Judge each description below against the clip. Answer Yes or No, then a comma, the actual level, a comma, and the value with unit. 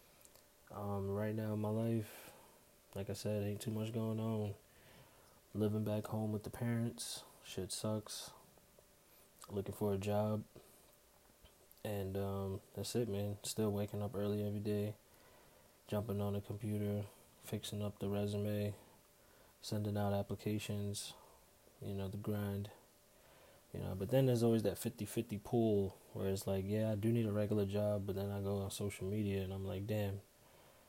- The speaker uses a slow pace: No, average, 160 wpm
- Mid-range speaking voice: No, low, 105 Hz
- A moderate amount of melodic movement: No, narrow, 1.3 semitones